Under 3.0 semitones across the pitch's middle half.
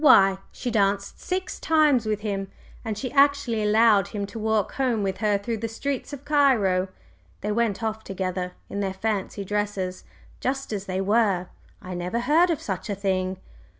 No: average, 3.6 semitones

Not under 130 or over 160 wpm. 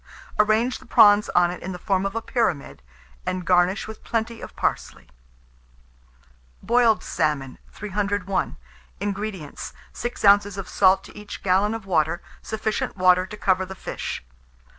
Yes: average, 145 wpm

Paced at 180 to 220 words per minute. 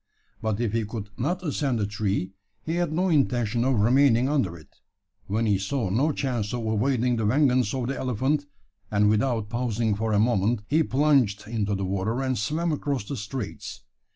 Yes: average, 185 wpm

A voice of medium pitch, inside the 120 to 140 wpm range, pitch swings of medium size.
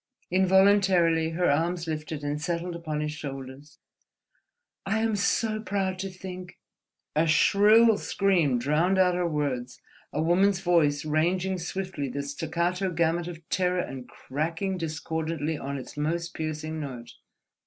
Yes: medium, 165 Hz; slow, 135 wpm; average, 3.6 semitones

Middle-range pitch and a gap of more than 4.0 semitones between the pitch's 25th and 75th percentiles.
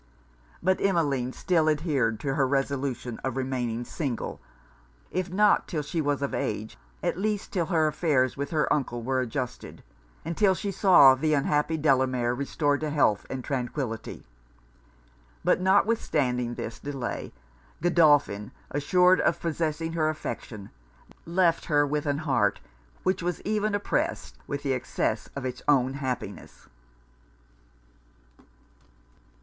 Yes: medium, 145 Hz; average, 4.4 semitones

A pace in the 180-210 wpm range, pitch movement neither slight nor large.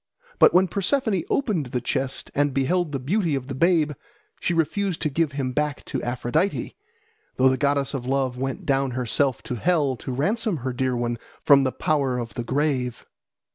Yes: average, 185 wpm; average, 4.3 semitones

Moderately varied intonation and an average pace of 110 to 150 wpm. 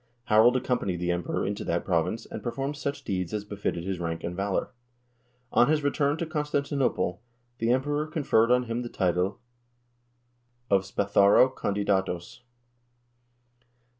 No: wide, 6.3 semitones; average, 140 wpm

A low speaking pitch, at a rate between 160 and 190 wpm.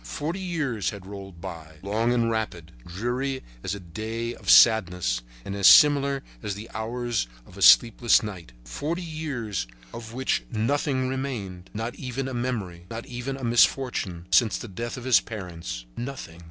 Yes: low, 115 Hz; average, 165 wpm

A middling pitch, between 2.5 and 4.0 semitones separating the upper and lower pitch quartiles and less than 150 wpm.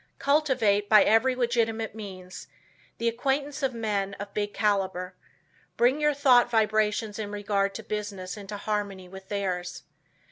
No: high, 210 Hz; average, 3.0 semitones; average, 140 wpm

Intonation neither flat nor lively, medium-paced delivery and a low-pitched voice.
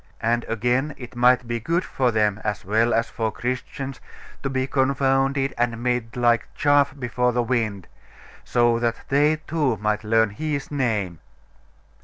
Yes: average, 3.0 semitones; average, 155 wpm; low, 120 Hz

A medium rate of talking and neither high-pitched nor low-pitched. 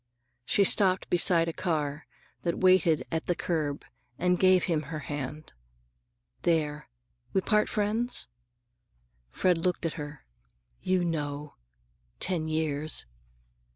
No: slow, 120 wpm; medium, 165 Hz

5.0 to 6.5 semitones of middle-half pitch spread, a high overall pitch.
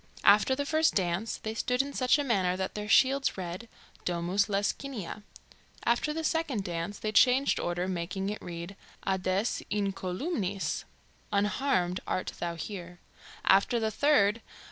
Yes: wide, 5.4 semitones; high, 200 Hz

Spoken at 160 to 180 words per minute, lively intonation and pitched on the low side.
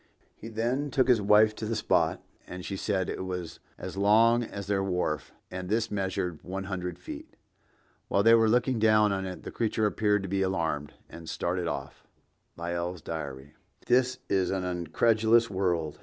No: average, 175 wpm; average, 3.6 semitones; very low, 95 Hz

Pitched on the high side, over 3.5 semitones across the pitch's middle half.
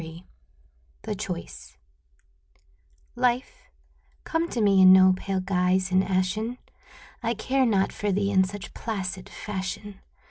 No: high, 195 Hz; average, 2.7 semitones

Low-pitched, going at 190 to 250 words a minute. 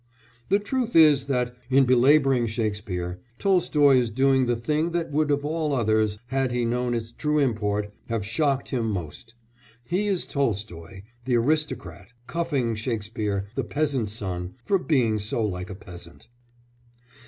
No: low, 120 Hz; average, 150 wpm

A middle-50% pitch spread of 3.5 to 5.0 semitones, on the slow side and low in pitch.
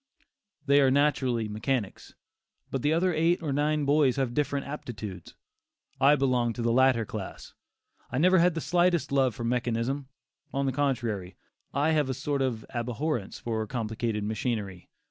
No: average, 4.0 semitones; average, 160 wpm; low, 130 Hz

